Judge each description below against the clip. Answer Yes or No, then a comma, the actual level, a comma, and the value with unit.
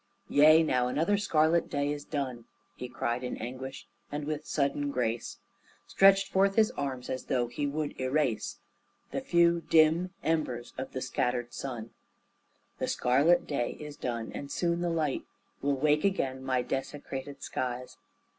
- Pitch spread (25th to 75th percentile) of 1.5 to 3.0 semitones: No, average, 3.8 semitones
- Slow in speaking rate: No, average, 155 wpm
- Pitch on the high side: No, medium, 140 Hz